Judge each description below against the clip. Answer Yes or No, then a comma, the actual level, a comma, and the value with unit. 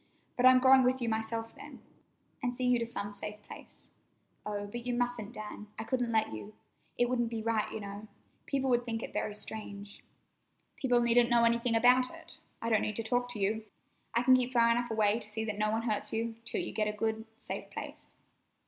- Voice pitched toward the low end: No, high, 230 Hz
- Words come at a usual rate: No, fast, 220 wpm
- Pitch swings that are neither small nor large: No, narrow, 2.3 semitones